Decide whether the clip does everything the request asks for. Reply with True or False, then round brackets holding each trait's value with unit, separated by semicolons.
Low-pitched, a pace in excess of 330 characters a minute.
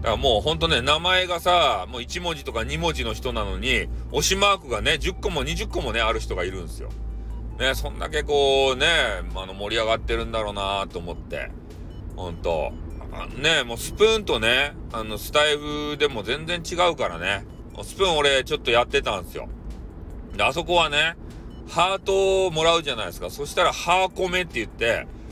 False (150 Hz; 365 characters per minute)